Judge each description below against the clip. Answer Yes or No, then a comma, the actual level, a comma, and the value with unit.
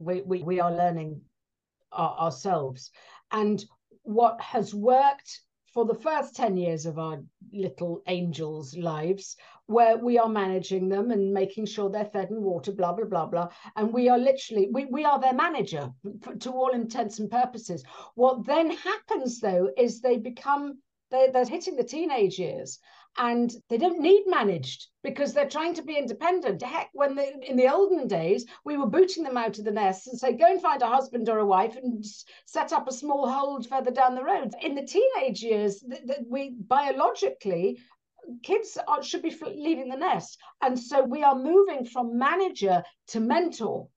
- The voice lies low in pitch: No, high, 245 Hz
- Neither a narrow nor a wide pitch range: No, wide, 5.8 semitones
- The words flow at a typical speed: Yes, average, 185 wpm